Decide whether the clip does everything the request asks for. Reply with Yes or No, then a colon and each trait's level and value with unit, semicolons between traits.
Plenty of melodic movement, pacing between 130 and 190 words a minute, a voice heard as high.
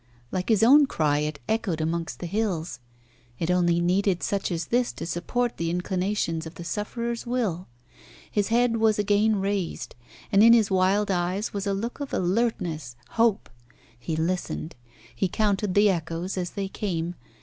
No: average, 4.1 semitones; average, 165 wpm; high, 195 Hz